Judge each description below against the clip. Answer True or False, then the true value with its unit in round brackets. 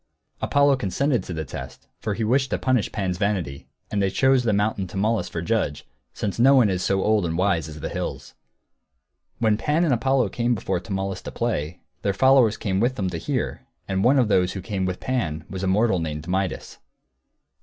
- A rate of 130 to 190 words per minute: False (205 wpm)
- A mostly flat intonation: False (4.5 semitones)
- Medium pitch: False (100 Hz)